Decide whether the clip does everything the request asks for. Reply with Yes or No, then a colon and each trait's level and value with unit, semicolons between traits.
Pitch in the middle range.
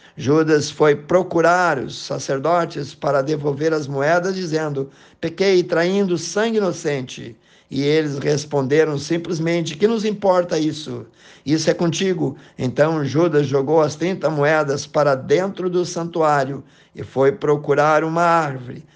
Yes: medium, 155 Hz